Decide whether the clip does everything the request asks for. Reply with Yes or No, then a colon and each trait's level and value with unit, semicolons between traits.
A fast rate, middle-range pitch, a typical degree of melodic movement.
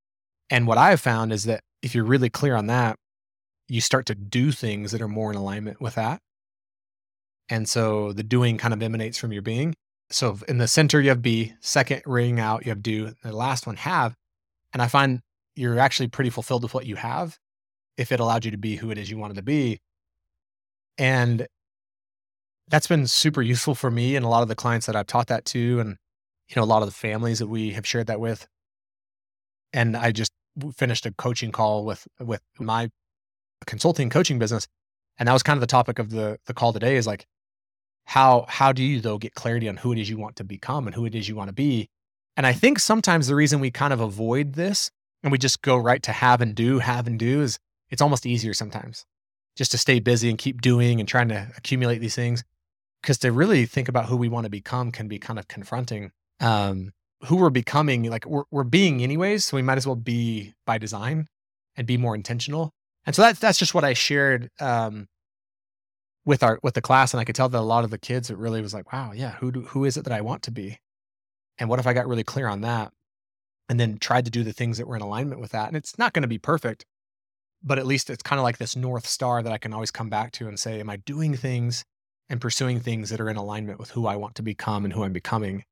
No: fast, 240 wpm; low, 115 Hz; average, 3.2 semitones